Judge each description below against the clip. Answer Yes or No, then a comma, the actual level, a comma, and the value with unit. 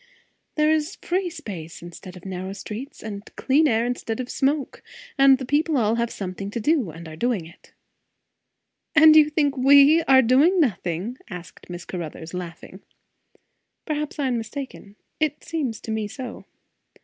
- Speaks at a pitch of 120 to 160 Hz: No, high, 245 Hz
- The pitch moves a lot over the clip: Yes, wide, 7.3 semitones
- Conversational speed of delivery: Yes, average, 160 wpm